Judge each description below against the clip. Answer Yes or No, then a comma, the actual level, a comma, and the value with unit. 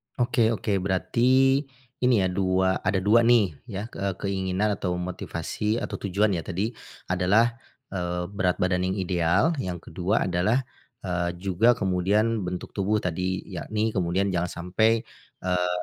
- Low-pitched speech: Yes, very low, 95 Hz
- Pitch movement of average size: Yes, average, 3.0 semitones